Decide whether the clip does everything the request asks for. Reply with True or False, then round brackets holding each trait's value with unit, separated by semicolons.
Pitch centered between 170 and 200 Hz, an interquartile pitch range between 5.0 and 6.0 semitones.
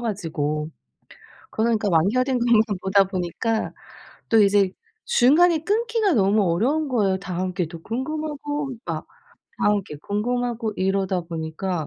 False (210 Hz; 5.5 semitones)